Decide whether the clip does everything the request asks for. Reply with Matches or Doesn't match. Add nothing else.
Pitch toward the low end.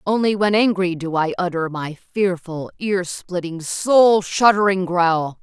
Doesn't match